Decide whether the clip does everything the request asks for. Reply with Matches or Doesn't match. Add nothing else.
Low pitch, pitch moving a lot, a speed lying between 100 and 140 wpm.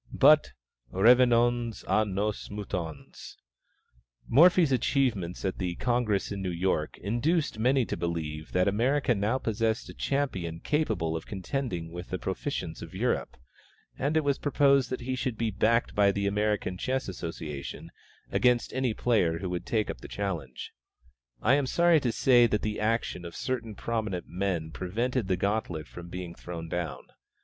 Doesn't match